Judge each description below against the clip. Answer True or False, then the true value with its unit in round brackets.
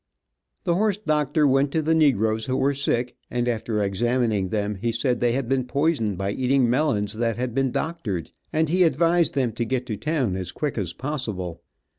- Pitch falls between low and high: False (125 Hz)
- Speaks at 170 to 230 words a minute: True (195 wpm)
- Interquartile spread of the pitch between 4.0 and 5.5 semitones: True (5.2 semitones)